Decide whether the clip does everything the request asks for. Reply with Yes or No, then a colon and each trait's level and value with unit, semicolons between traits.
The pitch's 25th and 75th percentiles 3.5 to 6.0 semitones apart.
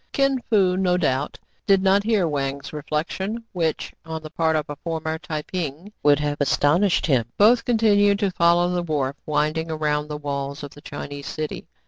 Yes: average, 4.4 semitones